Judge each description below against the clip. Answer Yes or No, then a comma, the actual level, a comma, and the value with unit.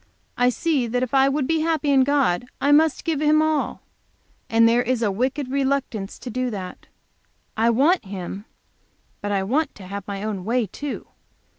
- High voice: Yes, very high, 255 Hz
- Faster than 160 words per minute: Yes, average, 185 wpm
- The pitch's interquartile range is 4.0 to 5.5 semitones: Yes, average, 5.2 semitones